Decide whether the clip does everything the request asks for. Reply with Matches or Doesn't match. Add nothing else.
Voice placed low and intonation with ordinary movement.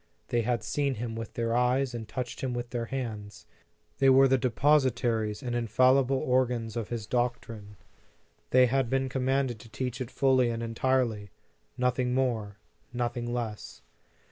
Doesn't match